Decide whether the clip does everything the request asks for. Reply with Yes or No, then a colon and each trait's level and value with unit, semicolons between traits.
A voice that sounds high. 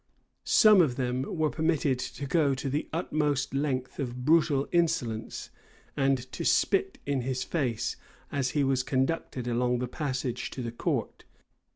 No: low, 135 Hz